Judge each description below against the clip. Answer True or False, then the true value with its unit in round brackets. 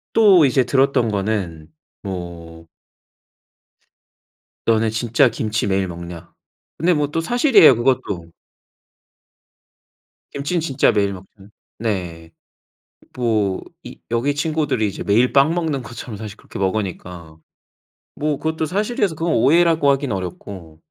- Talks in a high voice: False (115 Hz)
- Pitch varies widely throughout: True (7.5 semitones)